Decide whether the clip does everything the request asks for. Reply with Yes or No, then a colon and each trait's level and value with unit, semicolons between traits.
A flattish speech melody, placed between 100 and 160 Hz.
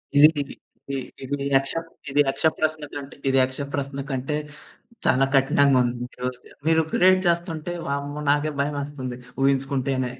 Yes: narrow, 1.8 semitones; medium, 140 Hz